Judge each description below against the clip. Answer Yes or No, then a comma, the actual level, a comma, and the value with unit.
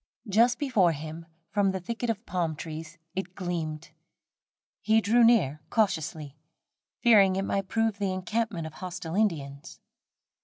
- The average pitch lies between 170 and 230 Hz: Yes, medium, 185 Hz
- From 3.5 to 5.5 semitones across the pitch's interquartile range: Yes, average, 5.2 semitones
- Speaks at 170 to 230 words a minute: No, average, 140 wpm